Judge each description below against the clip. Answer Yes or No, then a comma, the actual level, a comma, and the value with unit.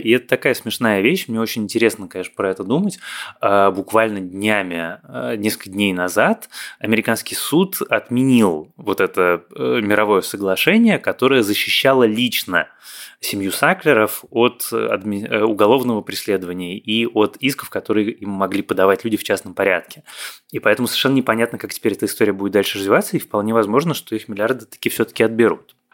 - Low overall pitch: Yes, low, 105 Hz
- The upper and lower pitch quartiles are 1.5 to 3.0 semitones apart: Yes, narrow, 2.6 semitones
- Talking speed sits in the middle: Yes, average, 145 wpm